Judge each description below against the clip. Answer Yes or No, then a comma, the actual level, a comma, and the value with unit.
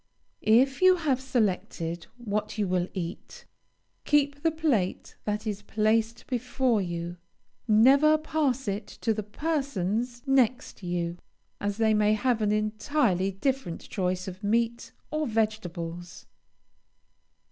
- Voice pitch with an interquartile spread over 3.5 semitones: Yes, wide, 5.5 semitones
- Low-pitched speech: No, high, 220 Hz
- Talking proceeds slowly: Yes, slow, 125 wpm